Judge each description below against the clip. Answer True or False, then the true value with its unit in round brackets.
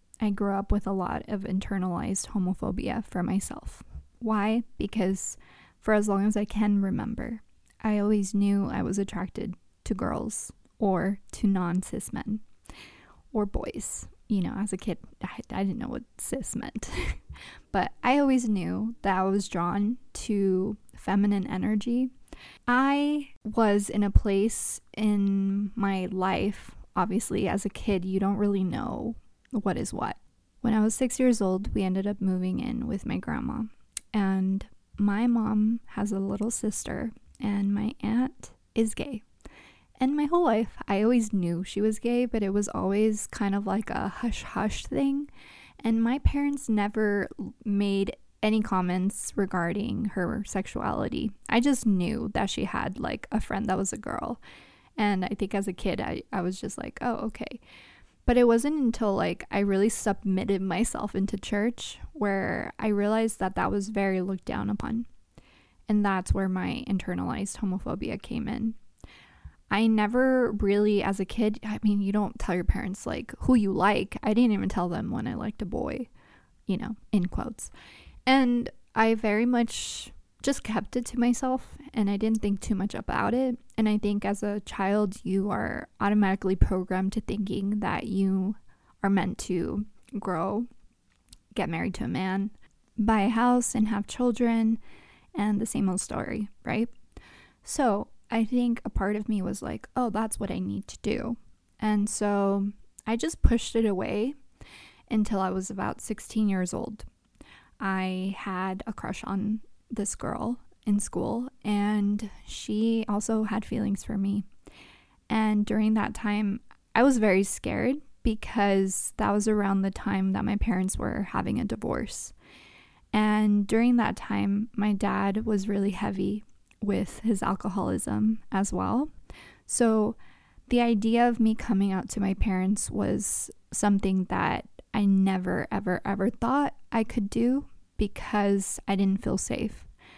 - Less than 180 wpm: True (160 wpm)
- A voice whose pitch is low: False (210 Hz)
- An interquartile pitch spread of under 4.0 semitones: True (2.4 semitones)